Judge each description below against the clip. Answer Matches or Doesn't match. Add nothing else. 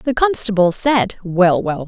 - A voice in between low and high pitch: Doesn't match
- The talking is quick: Doesn't match